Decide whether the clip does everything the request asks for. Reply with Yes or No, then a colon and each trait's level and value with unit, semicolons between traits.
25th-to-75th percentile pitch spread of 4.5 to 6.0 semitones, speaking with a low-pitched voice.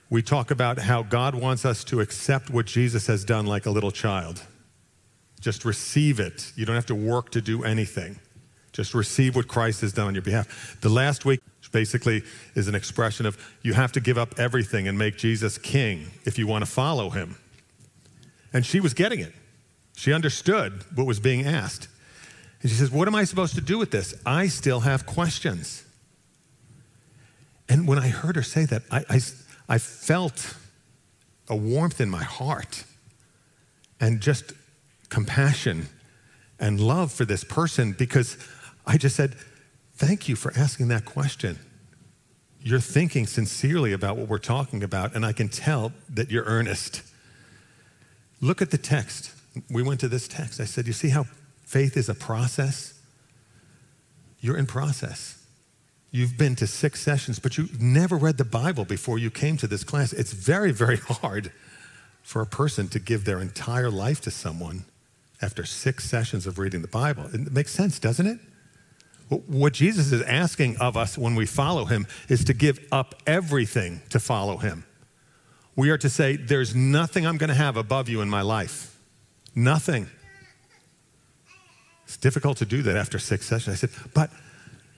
No: average, 3.9 semitones; low, 125 Hz